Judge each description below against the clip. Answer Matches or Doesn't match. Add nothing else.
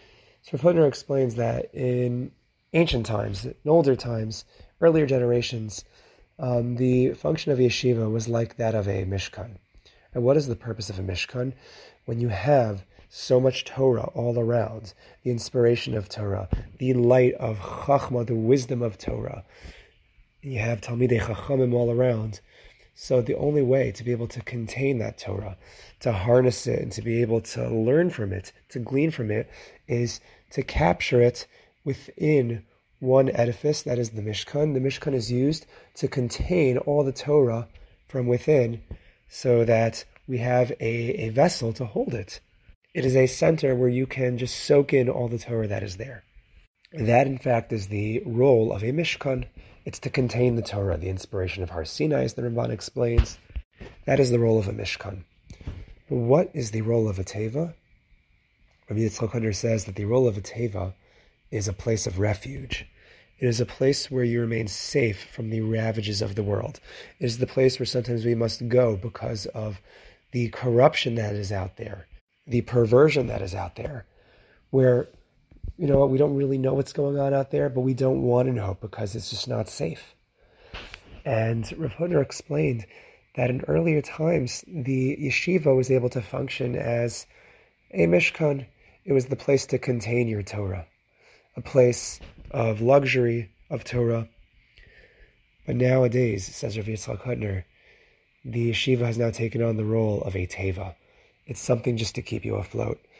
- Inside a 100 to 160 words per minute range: Doesn't match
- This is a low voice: Matches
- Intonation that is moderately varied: Matches